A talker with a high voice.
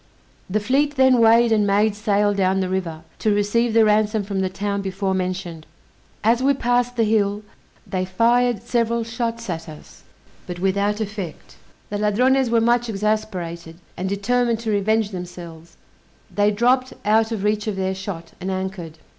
Yes: high, 210 Hz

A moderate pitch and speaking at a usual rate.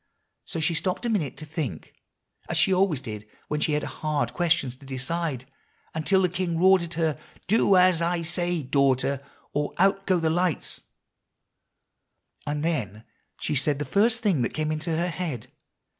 Yes: medium, 160 Hz; average, 175 wpm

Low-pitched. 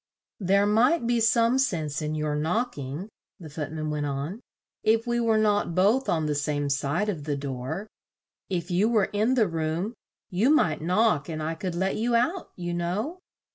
No: medium, 180 Hz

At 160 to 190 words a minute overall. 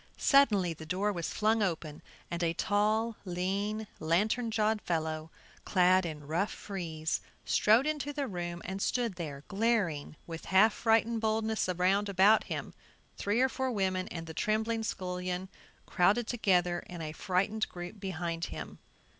No: average, 150 wpm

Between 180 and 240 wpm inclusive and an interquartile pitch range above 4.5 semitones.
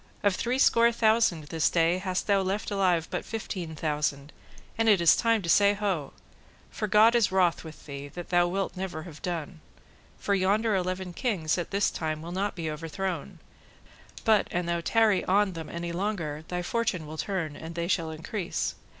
No: average, 185 wpm; average, 3.7 semitones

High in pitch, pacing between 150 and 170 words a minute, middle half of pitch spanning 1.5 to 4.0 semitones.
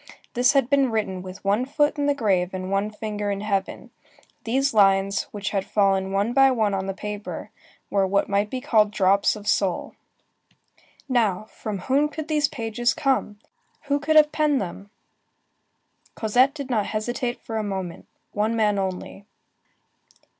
No: high, 210 Hz; average, 160 wpm; average, 4.7 semitones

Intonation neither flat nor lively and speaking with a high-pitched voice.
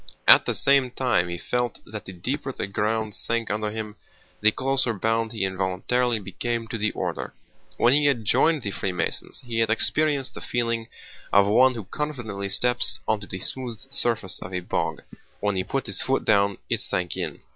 No: average, 3.7 semitones; low, 115 Hz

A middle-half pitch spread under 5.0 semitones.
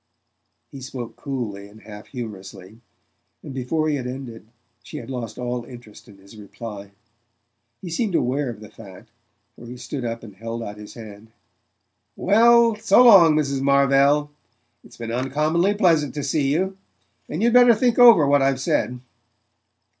No: average, 5.3 semitones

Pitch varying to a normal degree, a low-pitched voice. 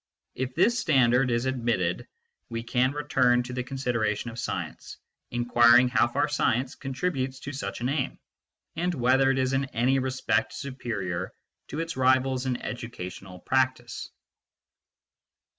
No: narrow, 2.1 semitones; low, 130 Hz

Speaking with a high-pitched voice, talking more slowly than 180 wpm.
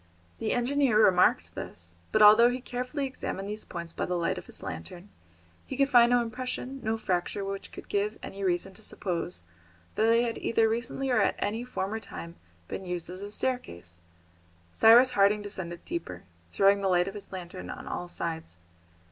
No: high, 205 Hz; average, 185 wpm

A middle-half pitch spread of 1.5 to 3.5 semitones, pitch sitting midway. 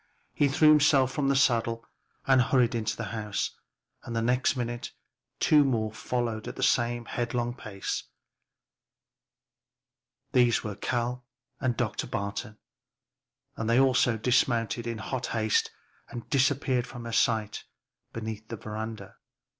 No: narrow, 2.4 semitones; low, 120 Hz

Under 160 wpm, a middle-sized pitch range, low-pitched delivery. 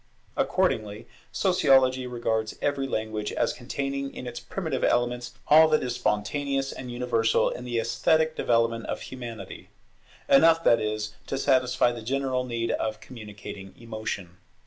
Yes: average, 140 wpm; average, 3.3 semitones; low, 120 Hz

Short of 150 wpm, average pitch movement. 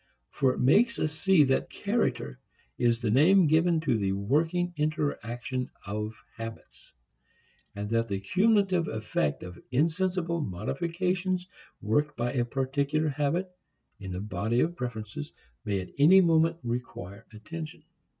No: slow, 135 wpm; wide, 7.3 semitones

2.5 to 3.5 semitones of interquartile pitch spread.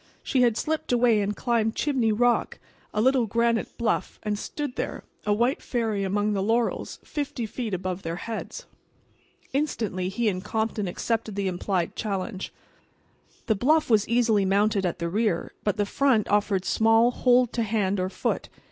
Yes: average, 3.2 semitones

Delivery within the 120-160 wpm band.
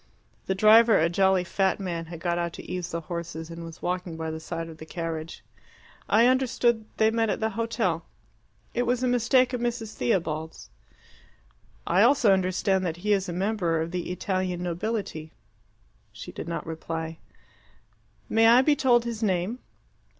No: average, 170 wpm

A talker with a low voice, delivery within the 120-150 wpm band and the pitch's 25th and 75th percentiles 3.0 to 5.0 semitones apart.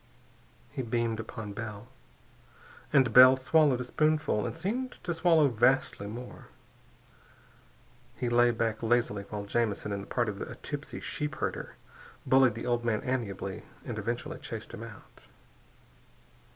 Yes: low, 120 Hz; average, 140 wpm; average, 3.5 semitones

